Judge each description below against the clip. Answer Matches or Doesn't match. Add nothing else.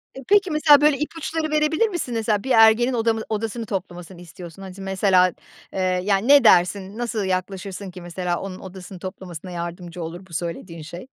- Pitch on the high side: Matches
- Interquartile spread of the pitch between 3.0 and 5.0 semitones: Matches